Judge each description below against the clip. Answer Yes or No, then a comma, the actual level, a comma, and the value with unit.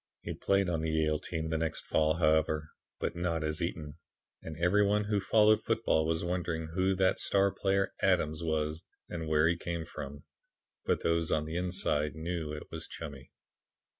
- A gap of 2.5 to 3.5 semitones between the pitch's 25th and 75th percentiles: Yes, average, 2.8 semitones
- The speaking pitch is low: Yes, very low, 80 Hz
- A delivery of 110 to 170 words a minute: No, average, 180 wpm